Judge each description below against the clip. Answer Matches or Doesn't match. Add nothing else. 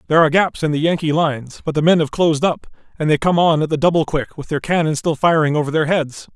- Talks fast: Matches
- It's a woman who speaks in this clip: Doesn't match